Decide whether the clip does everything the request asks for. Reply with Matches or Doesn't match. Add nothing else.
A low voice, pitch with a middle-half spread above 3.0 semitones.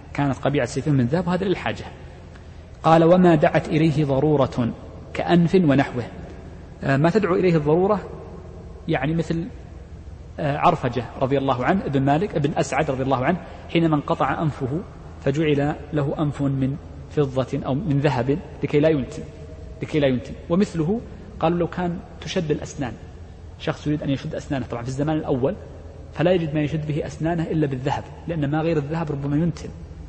Doesn't match